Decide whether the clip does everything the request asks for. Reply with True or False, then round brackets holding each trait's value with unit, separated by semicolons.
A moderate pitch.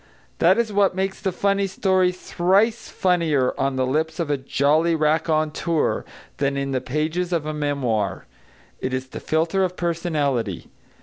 True (160 Hz)